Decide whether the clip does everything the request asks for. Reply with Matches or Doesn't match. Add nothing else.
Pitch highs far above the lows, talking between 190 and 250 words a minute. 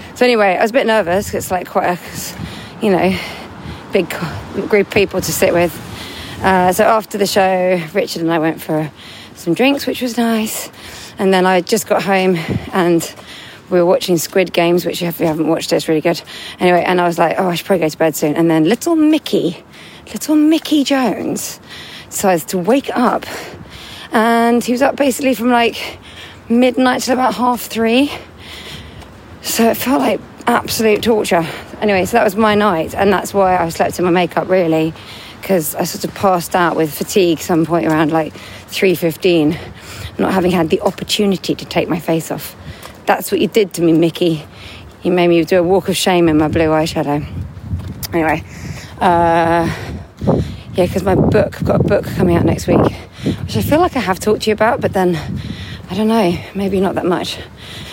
Doesn't match